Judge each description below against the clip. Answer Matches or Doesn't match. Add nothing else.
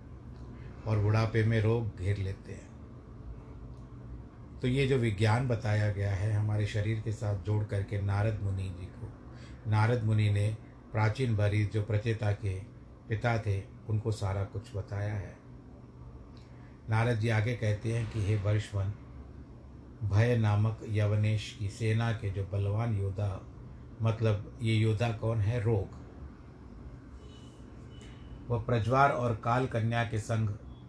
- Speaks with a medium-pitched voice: Doesn't match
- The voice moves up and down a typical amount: Doesn't match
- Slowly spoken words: Doesn't match